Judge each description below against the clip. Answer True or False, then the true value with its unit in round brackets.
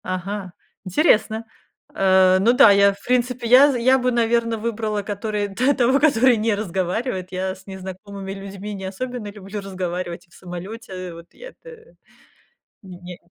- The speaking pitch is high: True (205 Hz)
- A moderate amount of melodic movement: True (3.9 semitones)